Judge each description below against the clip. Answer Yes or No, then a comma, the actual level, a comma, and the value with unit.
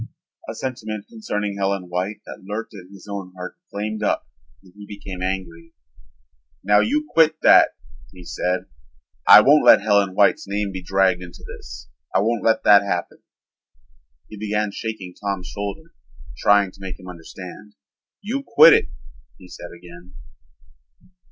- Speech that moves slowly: No, average, 150 wpm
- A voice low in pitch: Yes, low, 100 Hz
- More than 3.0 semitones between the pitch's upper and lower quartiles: No, narrow, 2.5 semitones